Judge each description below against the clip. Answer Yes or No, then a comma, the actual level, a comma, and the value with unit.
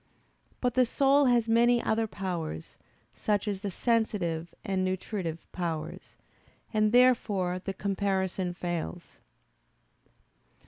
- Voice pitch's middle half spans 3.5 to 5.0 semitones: Yes, average, 4.3 semitones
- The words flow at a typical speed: No, slow, 105 wpm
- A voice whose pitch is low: No, high, 195 Hz